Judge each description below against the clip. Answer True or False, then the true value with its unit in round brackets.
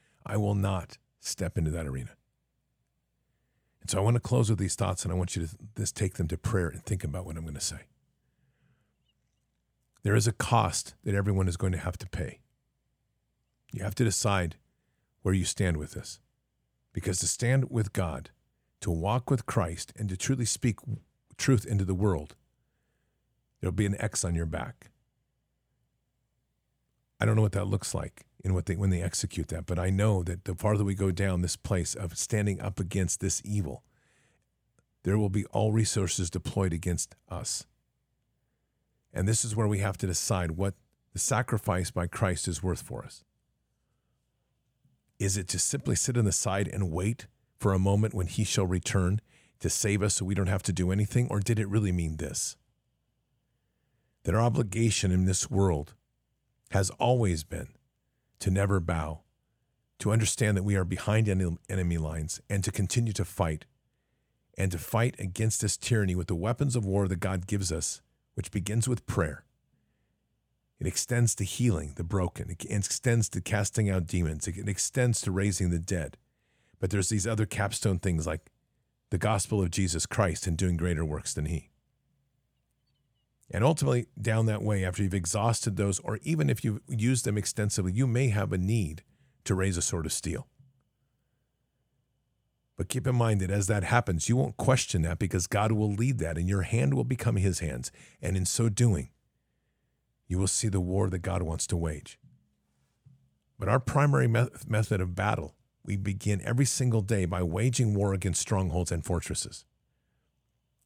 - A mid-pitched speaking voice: False (100 Hz)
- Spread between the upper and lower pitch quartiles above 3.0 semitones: True (4.3 semitones)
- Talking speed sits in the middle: True (180 wpm)